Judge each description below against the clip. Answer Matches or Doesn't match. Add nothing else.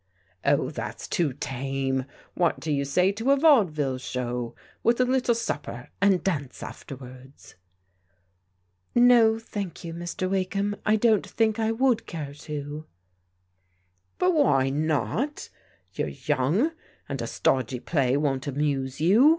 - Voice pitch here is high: Doesn't match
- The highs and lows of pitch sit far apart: Matches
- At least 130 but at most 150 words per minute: Matches